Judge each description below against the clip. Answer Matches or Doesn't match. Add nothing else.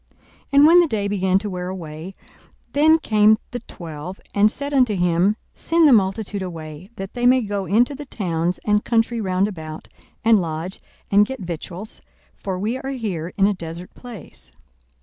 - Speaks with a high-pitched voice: Matches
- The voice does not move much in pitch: Doesn't match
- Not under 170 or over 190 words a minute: Matches